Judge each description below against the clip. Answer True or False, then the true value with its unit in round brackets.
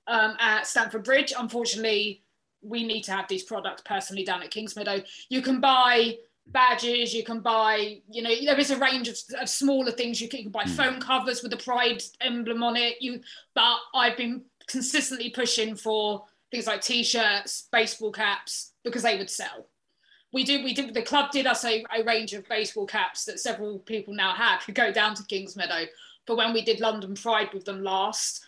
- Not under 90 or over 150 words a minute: False (200 wpm)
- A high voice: True (230 Hz)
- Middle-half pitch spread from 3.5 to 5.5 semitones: False (2.7 semitones)